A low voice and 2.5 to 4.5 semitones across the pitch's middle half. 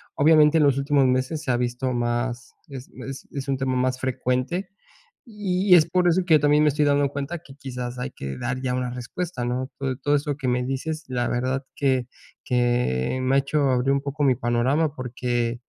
Yes: low, 130 Hz; average, 2.8 semitones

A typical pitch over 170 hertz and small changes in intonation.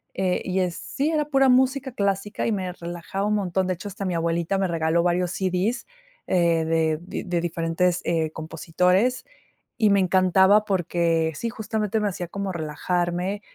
No: medium, 185 Hz; average, 3.1 semitones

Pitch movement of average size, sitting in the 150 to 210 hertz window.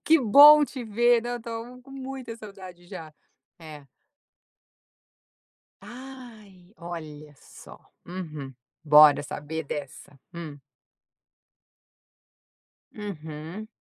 No: wide, 7.7 semitones; medium, 185 Hz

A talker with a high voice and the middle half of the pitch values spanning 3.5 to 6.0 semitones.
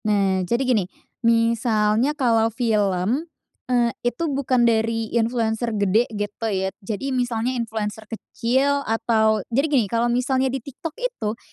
No: high, 230 Hz; average, 2.7 semitones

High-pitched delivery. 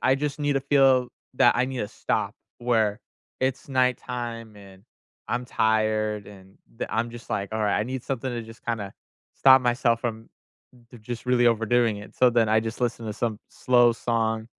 No: low, 115 Hz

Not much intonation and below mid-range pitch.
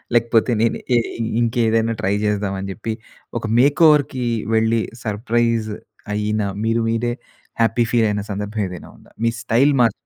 Yes: narrow, 1.9 semitones; low, 115 Hz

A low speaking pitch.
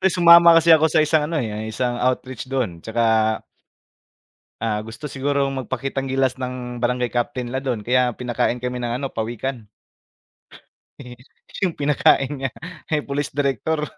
Yes: low, 130 Hz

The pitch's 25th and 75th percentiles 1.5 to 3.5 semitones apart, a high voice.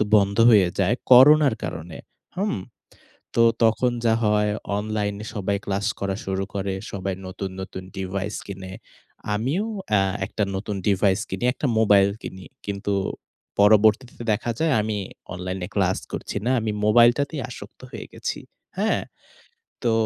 No: average, 2.8 semitones; low, 105 Hz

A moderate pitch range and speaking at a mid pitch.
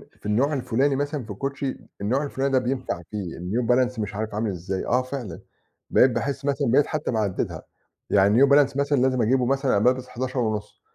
No: average, 4.2 semitones; low, 125 Hz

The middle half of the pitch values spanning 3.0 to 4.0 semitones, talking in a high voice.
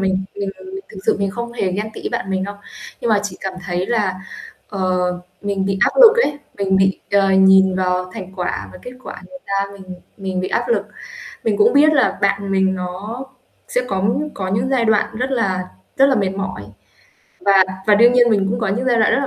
Yes: average, 3.3 semitones; high, 200 Hz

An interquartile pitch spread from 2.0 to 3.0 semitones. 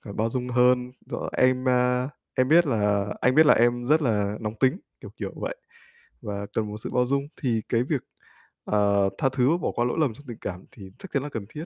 No: average, 3.9 semitones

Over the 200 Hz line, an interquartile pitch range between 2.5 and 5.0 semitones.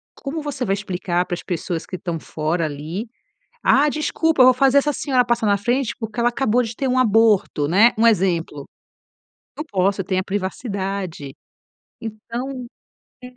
No: high, 215 Hz; wide, 5.5 semitones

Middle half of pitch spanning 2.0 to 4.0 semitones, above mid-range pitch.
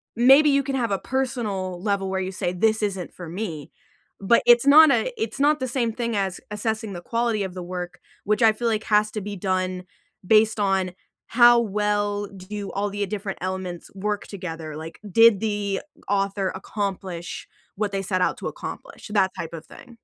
Yes: average, 2.9 semitones; high, 205 Hz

